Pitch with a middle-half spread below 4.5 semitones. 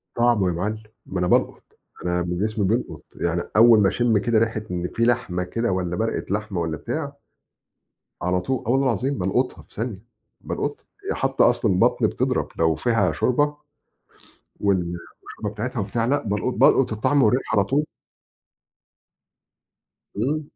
No: average, 5.0 semitones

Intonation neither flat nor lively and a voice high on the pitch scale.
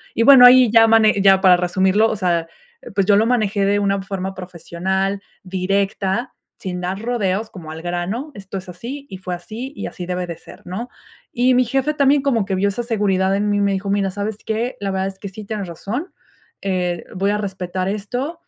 Yes: average, 3.2 semitones; high, 200 Hz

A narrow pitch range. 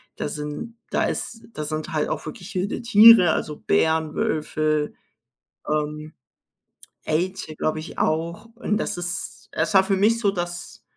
No: average, 4.3 semitones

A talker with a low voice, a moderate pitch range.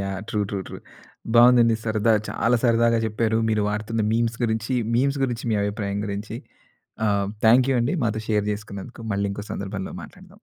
No: low, 110 Hz; narrow, 2.2 semitones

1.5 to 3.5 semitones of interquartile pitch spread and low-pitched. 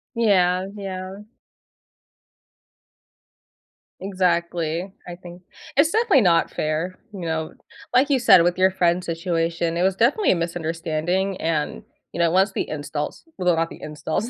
No: narrow, 2.5 semitones; medium, 180 Hz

